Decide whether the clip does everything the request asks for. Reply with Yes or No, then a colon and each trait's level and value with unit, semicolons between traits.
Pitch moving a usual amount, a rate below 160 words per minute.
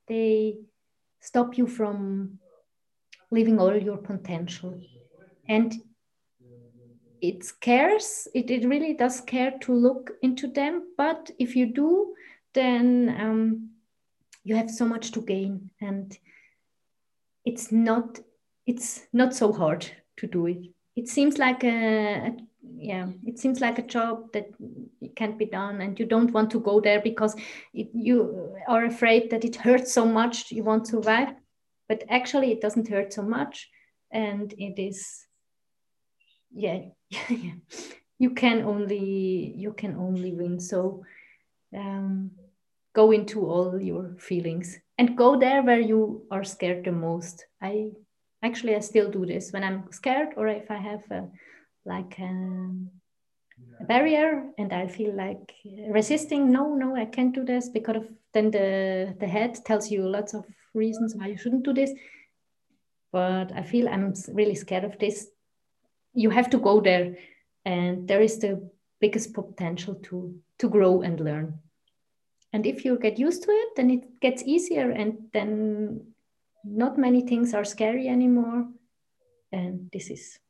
Yes: average, 4.0 semitones; average, 150 wpm